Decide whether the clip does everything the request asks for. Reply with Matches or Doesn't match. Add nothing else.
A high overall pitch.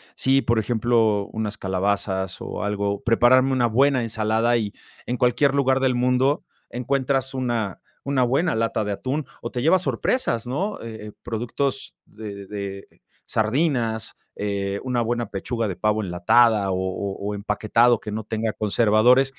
Doesn't match